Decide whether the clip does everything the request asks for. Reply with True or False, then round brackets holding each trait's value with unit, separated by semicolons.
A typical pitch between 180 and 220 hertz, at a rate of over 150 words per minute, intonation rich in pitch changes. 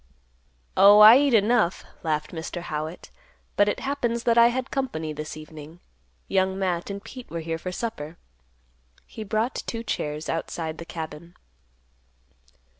False (185 Hz; 145 wpm; 6.3 semitones)